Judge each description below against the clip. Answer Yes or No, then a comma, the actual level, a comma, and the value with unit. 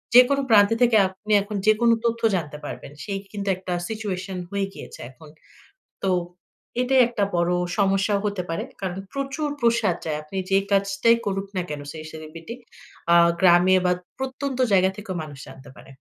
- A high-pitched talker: Yes, high, 195 Hz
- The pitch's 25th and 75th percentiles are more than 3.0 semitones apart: Yes, average, 4.2 semitones